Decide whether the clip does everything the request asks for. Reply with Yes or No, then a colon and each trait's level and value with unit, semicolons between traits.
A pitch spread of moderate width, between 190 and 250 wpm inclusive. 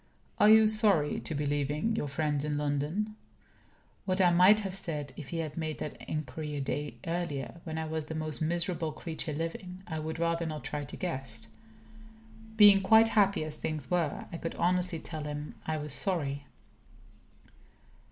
No: average, 3.4 semitones; average, 175 wpm